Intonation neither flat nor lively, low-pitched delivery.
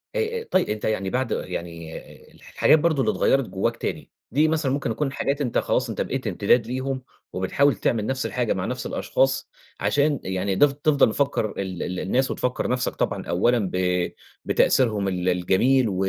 No: wide, 6.5 semitones; low, 125 Hz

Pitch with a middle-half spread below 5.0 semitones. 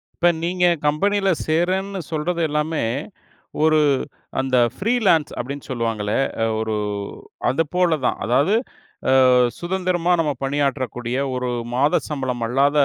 No: wide, 5.4 semitones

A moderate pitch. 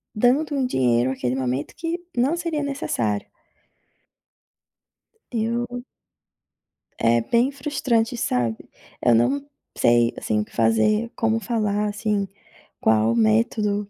No: high, 210 Hz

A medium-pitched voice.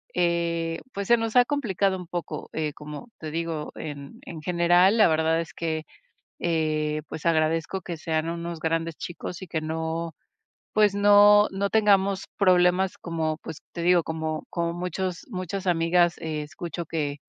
Yes: medium, 170 Hz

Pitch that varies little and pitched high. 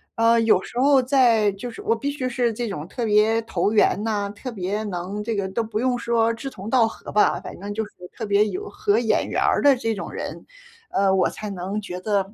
No: average, 3.2 semitones; high, 220 Hz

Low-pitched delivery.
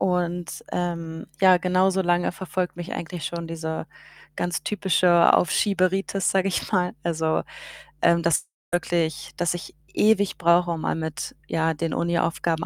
No: medium, 175 Hz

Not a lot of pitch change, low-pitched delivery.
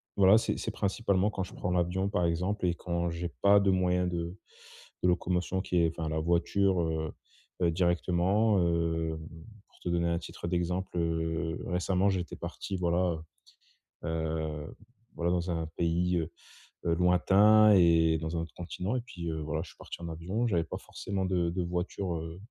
Yes: narrow, 2.0 semitones; very low, 85 Hz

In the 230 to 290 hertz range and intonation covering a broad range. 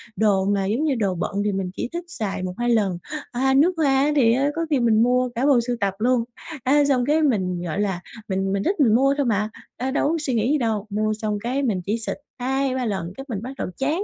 No: high, 240 Hz; average, 4.9 semitones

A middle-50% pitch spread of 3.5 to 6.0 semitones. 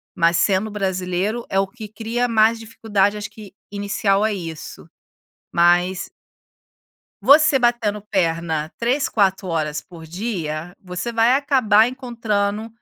Yes: average, 4.0 semitones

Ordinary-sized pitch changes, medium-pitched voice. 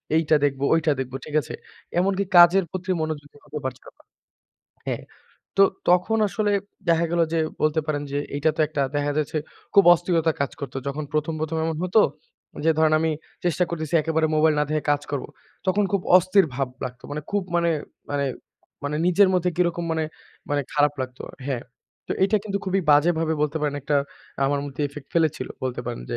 Yes: average, 3.2 semitones; medium, 155 Hz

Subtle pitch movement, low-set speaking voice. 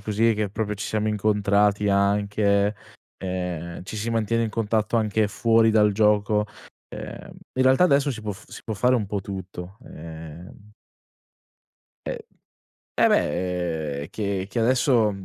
Yes: narrow, 2.2 semitones; low, 105 Hz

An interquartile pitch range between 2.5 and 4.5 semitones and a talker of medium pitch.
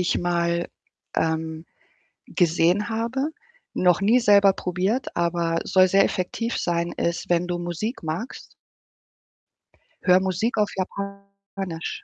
Yes: average, 2.8 semitones; medium, 180 Hz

